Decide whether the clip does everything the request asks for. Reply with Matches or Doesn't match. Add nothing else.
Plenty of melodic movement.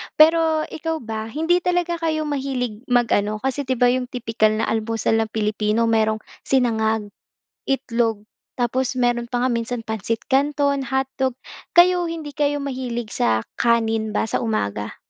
Doesn't match